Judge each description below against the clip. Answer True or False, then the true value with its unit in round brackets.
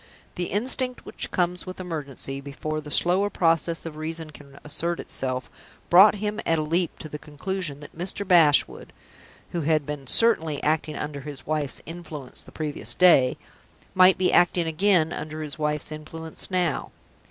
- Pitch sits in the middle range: True (160 Hz)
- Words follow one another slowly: False (165 wpm)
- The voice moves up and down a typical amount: True (3.2 semitones)